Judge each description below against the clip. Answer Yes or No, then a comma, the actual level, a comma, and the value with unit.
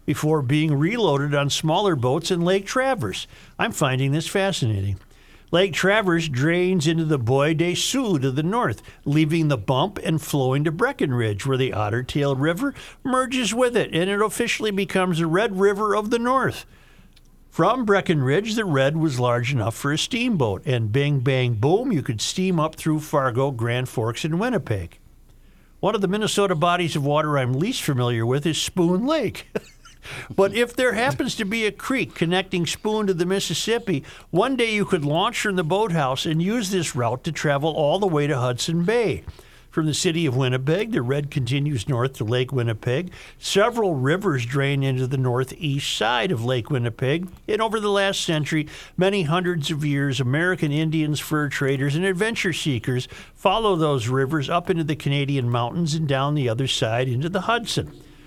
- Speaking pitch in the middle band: Yes, medium, 155 Hz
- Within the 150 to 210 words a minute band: Yes, average, 180 wpm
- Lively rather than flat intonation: Yes, wide, 5.9 semitones